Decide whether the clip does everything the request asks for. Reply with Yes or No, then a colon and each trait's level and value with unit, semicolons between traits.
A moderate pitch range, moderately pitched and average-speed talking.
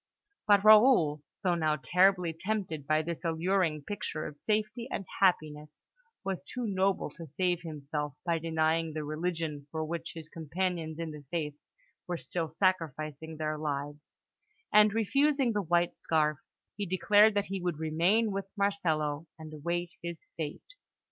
Yes: average, 4.0 semitones; medium, 165 Hz; average, 150 wpm